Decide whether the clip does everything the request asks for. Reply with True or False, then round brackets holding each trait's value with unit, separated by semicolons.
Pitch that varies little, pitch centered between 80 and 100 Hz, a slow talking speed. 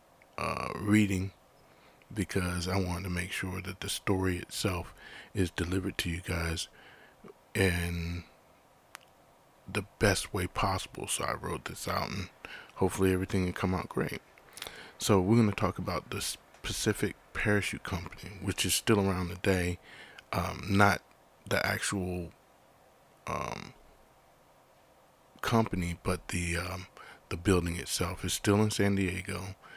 True (1.9 semitones; 95 Hz; 130 wpm)